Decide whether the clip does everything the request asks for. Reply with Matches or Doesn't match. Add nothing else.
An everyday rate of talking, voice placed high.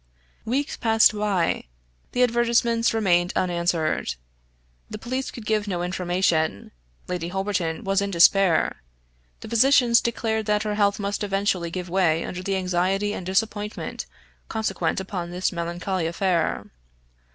Doesn't match